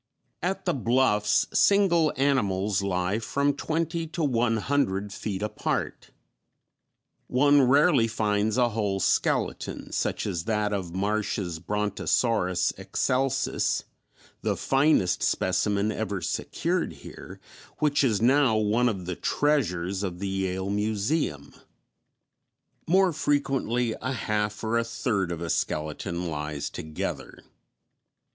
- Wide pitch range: Yes, wide, 5.9 semitones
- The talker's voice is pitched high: No, low, 110 Hz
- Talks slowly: Yes, slow, 120 wpm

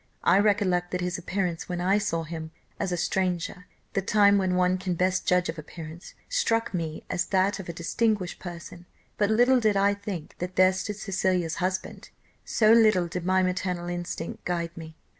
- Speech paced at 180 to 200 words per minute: Yes, average, 185 wpm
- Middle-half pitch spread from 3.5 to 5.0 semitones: No, narrow, 2.4 semitones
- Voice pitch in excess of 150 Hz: Yes, medium, 185 Hz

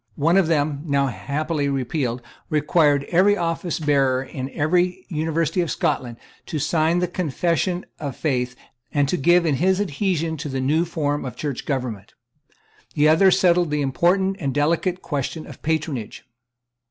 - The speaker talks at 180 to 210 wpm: No, average, 155 wpm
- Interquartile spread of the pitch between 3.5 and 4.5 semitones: Yes, average, 3.8 semitones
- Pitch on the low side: No, medium, 155 Hz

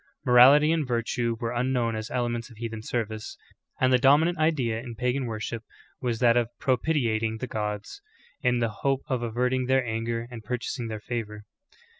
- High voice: No, low, 120 Hz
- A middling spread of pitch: No, narrow, 2.2 semitones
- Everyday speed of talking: Yes, average, 175 wpm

